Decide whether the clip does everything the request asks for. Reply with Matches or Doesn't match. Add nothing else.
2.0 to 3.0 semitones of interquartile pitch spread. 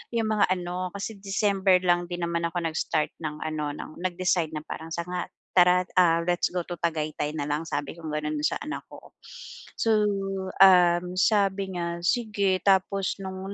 Matches